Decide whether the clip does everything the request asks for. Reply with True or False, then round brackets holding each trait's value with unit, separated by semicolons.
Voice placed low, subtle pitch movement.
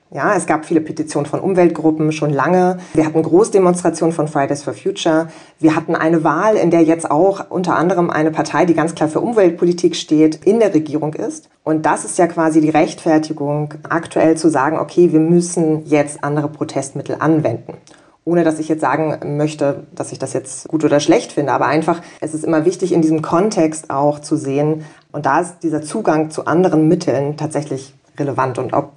False (155 Hz; 2.3 semitones)